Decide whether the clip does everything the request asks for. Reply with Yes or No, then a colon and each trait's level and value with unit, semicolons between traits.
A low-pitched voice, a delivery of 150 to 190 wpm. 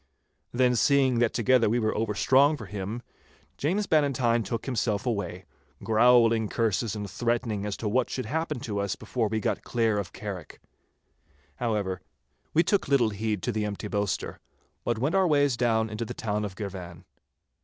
Yes: low, 115 Hz; average, 170 wpm